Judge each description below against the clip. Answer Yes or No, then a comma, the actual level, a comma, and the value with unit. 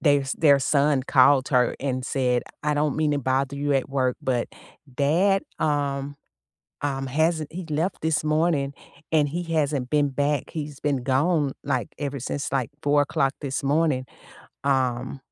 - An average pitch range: No, narrow, 2.0 semitones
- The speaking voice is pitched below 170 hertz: Yes, medium, 140 Hz